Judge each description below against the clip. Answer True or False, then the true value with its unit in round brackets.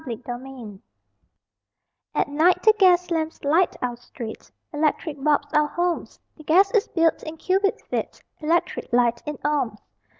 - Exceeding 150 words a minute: False (145 wpm)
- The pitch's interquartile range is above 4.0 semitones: True (5.1 semitones)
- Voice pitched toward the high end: True (305 Hz)